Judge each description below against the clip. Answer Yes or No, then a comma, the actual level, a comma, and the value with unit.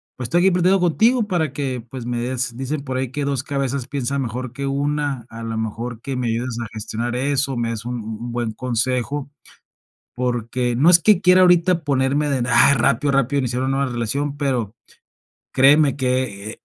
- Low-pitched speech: Yes, low, 130 Hz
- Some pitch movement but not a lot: Yes, average, 3.1 semitones